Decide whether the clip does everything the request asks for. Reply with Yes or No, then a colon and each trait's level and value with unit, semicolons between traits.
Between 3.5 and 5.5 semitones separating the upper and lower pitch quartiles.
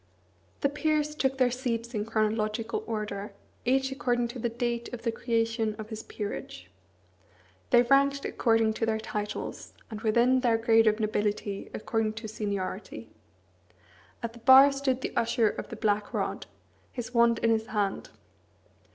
No: narrow, 2.4 semitones